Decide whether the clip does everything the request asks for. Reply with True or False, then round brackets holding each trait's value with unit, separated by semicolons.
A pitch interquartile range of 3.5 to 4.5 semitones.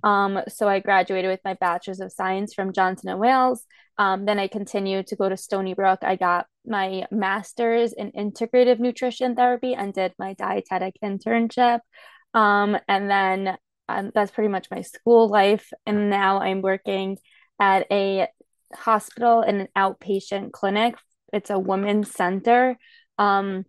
False (3.1 semitones)